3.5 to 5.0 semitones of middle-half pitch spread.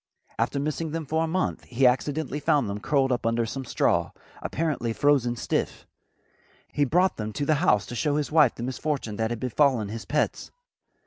Yes: average, 4.3 semitones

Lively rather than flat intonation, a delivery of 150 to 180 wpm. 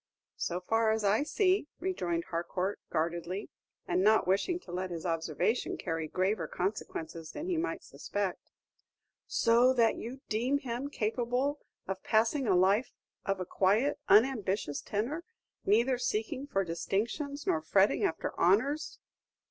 No: wide, 5.9 semitones; average, 140 wpm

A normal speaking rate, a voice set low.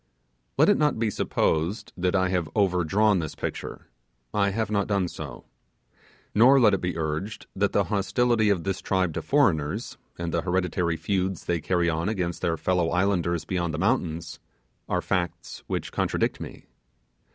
Yes: average, 165 wpm; very low, 90 Hz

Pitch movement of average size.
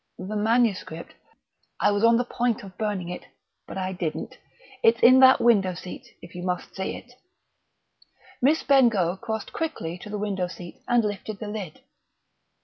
Yes: average, 4.2 semitones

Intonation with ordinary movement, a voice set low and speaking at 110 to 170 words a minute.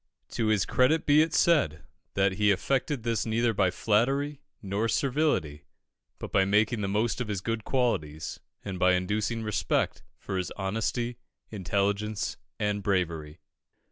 Yes: average, 3.7 semitones; low, 105 Hz; average, 145 wpm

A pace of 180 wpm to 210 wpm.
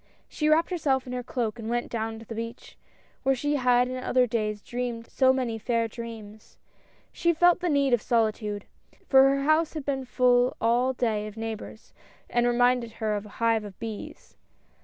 Yes: average, 195 wpm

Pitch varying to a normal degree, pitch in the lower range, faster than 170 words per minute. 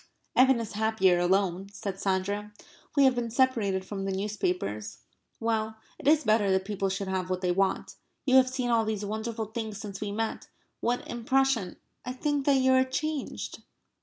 No: average, 4.4 semitones; high, 215 Hz; average, 180 wpm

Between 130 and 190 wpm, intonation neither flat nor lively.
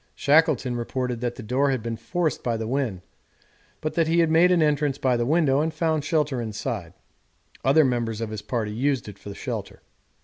No: average, 200 wpm; average, 4.9 semitones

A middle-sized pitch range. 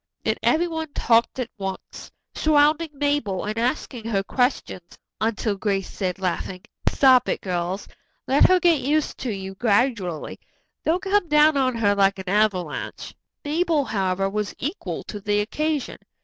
No: wide, 7.1 semitones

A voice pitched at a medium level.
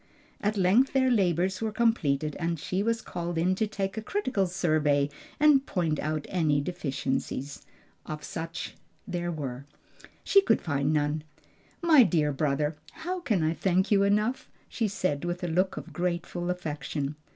Yes: medium, 175 Hz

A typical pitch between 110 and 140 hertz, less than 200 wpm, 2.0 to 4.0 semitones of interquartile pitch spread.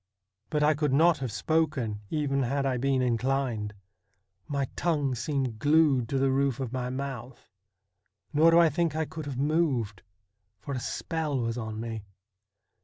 Yes: low, 135 Hz; average, 165 wpm; average, 3.7 semitones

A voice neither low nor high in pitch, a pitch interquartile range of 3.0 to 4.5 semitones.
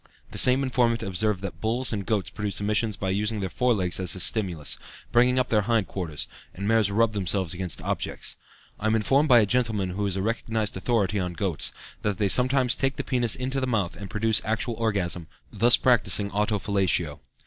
No: low, 105 Hz; average, 3.4 semitones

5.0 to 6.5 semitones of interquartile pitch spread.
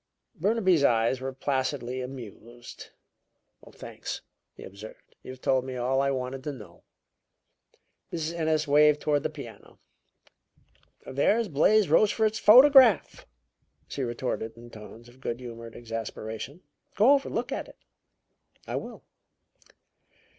Yes: wide, 5.4 semitones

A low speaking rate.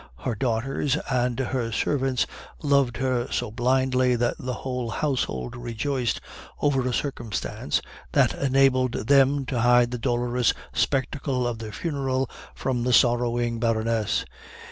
Yes: slow, 130 wpm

